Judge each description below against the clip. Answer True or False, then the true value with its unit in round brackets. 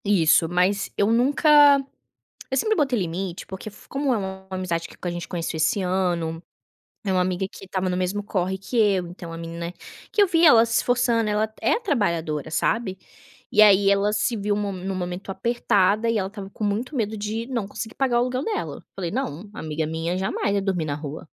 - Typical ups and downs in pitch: True (4.1 semitones)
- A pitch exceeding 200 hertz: False (195 Hz)